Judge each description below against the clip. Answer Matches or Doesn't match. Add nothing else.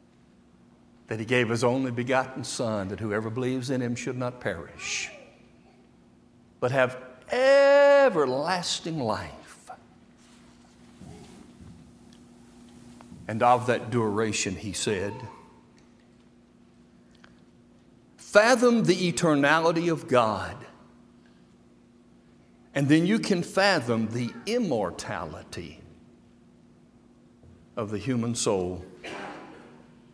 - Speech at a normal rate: Doesn't match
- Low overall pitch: Matches